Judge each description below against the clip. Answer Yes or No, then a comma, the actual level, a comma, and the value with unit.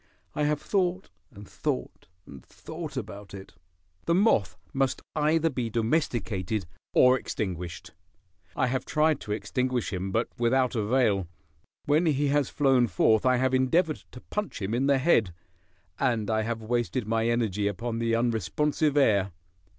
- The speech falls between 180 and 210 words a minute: No, average, 150 wpm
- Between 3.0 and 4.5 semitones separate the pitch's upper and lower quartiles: No, average, 5.0 semitones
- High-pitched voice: No, low, 120 Hz